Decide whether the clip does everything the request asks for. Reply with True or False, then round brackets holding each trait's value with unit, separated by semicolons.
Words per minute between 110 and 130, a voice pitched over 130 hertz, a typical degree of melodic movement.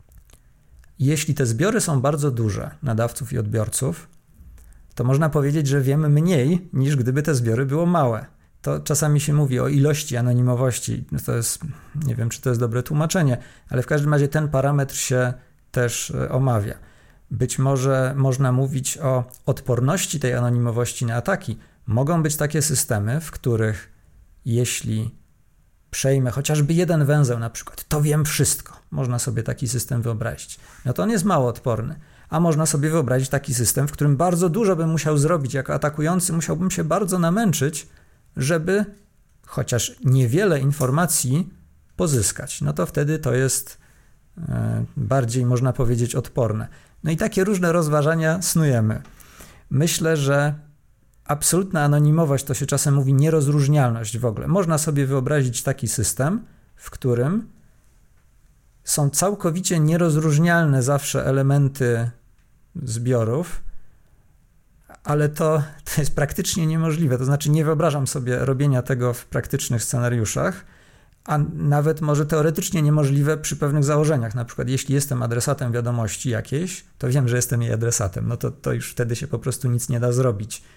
False (145 wpm; 140 Hz; 4.0 semitones)